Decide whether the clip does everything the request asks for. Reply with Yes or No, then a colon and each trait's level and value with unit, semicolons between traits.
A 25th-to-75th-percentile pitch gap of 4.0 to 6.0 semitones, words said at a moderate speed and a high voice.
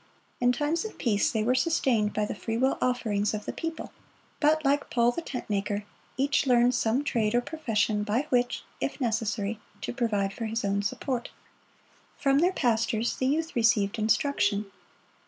Yes: average, 4.3 semitones; average, 170 wpm; high, 235 Hz